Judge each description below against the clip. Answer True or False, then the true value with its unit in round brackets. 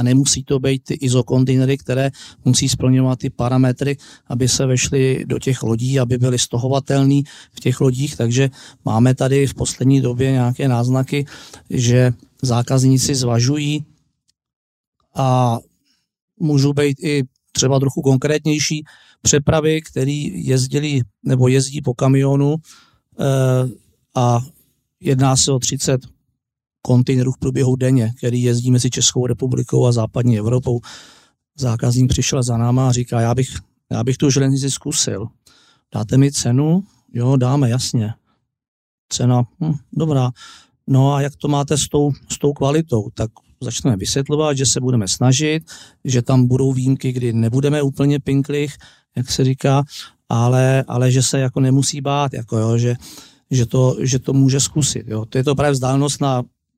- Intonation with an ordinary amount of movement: False (1.9 semitones)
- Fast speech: False (145 wpm)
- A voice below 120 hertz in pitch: False (130 Hz)